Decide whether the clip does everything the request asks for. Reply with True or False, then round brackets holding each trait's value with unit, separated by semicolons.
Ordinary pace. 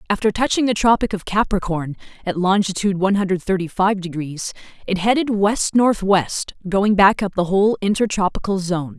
True (160 wpm)